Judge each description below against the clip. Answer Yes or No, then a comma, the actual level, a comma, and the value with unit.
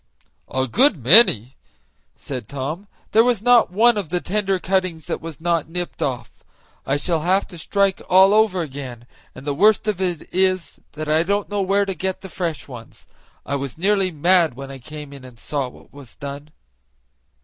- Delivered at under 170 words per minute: No, average, 195 wpm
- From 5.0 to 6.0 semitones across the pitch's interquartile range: Yes, wide, 5.5 semitones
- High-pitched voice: No, medium, 170 Hz